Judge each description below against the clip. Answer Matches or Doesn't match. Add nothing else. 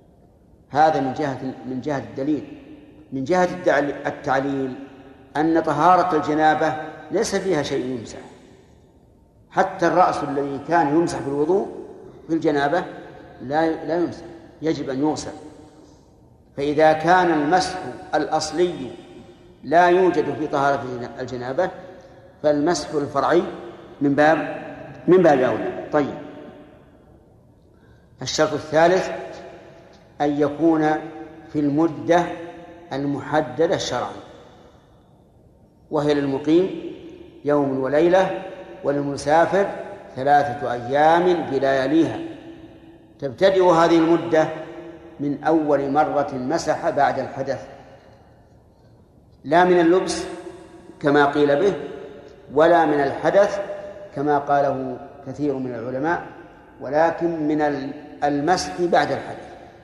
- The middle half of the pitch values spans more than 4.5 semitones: Doesn't match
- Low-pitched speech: Doesn't match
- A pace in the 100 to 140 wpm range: Doesn't match